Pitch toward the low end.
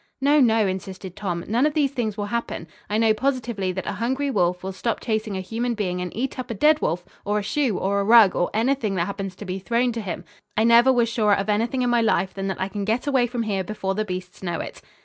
No: high, 215 Hz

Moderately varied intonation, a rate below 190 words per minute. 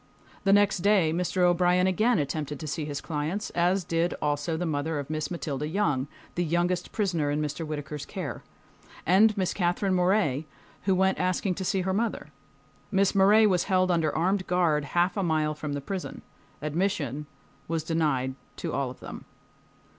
Yes: average, 3.8 semitones; average, 175 wpm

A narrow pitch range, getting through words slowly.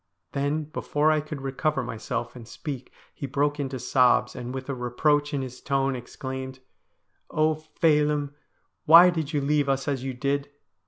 No: narrow, 2.3 semitones; average, 170 wpm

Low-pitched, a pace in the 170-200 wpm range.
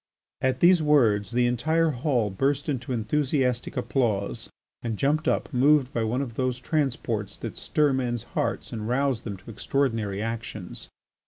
No: low, 125 Hz; average, 155 wpm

